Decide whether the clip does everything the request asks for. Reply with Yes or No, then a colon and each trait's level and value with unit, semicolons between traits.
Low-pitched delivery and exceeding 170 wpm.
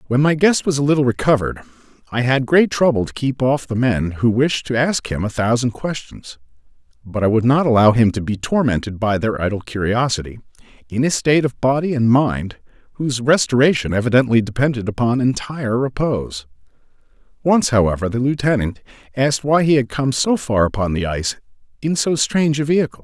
Yes: low, 125 Hz; average, 180 wpm